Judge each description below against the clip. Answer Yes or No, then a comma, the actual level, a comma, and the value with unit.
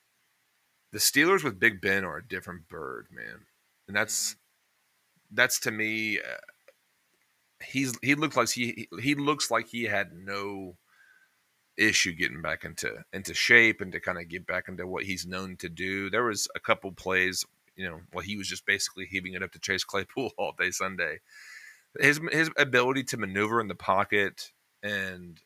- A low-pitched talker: Yes, low, 100 Hz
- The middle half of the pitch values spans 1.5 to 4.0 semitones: No, average, 4.7 semitones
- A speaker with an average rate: Yes, average, 175 wpm